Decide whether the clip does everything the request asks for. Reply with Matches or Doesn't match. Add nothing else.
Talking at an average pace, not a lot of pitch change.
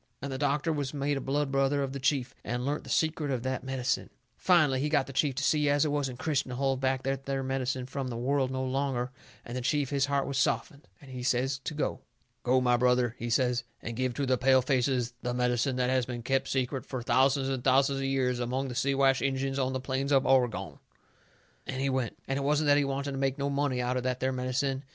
Doesn't match